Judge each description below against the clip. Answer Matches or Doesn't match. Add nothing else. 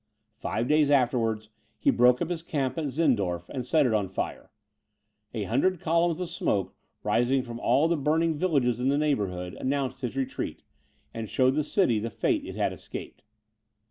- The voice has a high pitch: Doesn't match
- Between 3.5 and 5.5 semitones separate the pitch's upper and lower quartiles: Matches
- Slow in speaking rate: Doesn't match